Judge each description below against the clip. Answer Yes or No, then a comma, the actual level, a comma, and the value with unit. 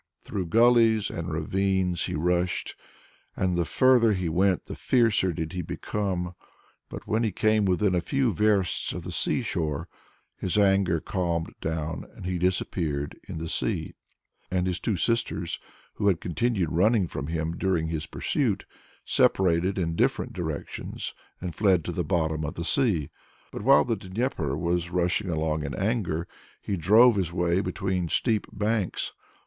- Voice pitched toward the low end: Yes, very low, 90 Hz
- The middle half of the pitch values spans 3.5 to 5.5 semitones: Yes, average, 3.8 semitones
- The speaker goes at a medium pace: Yes, average, 160 wpm